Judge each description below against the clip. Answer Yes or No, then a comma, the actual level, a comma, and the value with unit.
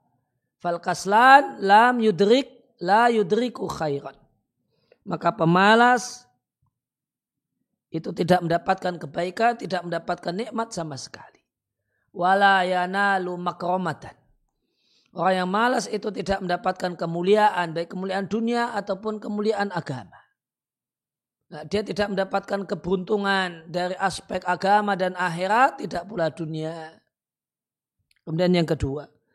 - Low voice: No, medium, 185 Hz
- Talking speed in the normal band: Yes, average, 95 wpm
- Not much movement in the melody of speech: No, average, 3.6 semitones